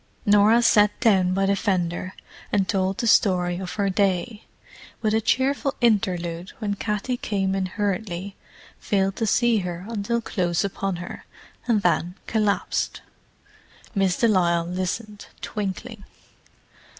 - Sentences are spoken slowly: Yes, slow, 130 wpm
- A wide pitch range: No, average, 2.9 semitones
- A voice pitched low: No, high, 200 Hz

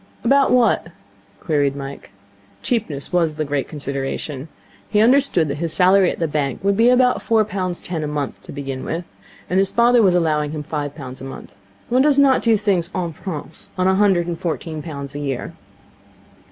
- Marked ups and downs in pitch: Yes, wide, 5.8 semitones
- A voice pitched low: No, medium, 170 Hz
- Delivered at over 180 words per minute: Yes, average, 195 wpm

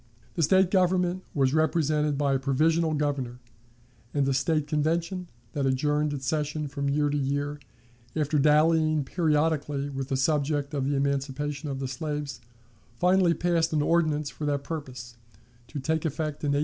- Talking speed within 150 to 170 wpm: Yes, average, 160 wpm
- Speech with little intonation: Yes, narrow, 2.2 semitones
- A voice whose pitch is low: No, medium, 150 Hz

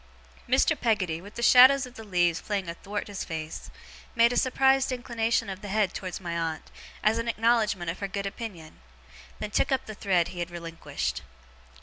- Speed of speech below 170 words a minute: No, average, 190 wpm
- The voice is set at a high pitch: Yes, high, 205 Hz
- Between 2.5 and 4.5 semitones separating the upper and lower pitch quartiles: No, average, 5.1 semitones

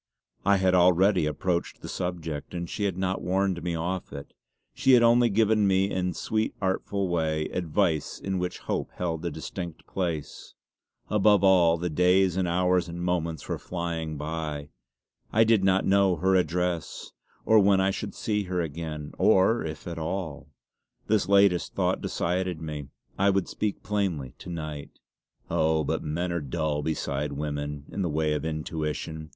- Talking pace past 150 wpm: Yes, average, 170 wpm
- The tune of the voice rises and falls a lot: No, average, 3.4 semitones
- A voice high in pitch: No, very low, 90 Hz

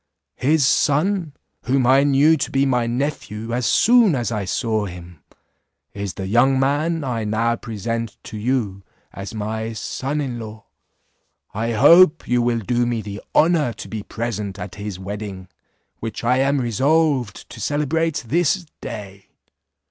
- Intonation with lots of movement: No, average, 4.9 semitones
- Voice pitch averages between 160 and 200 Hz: No, low, 120 Hz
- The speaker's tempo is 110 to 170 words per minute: Yes, average, 155 wpm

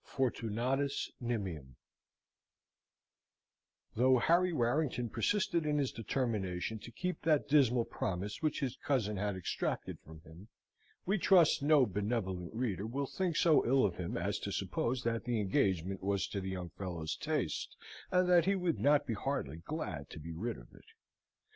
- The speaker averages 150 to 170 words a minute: Yes, average, 160 wpm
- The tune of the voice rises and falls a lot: Yes, wide, 7.4 semitones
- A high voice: No, low, 120 Hz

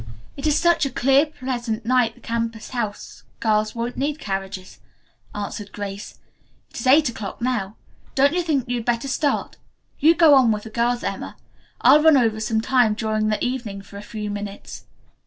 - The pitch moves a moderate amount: Yes, average, 3.8 semitones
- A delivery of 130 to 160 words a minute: No, average, 185 wpm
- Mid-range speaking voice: No, high, 235 Hz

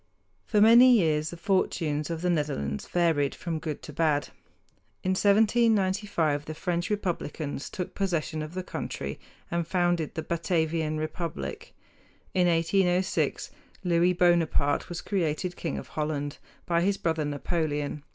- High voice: No, medium, 170 Hz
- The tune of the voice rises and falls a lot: No, average, 3.0 semitones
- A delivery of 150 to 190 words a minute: No, slow, 135 wpm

